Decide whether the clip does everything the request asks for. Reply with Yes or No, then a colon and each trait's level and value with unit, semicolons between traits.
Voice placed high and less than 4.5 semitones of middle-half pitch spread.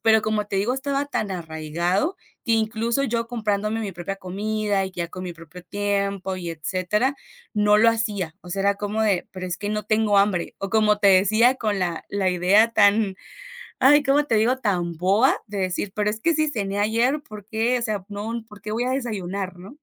Yes: high, 210 Hz; average, 3.0 semitones